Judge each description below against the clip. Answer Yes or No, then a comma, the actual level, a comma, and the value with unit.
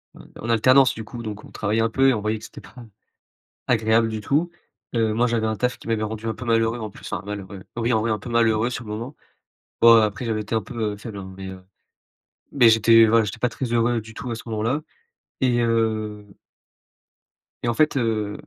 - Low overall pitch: Yes, low, 115 Hz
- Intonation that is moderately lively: No, narrow, 1.6 semitones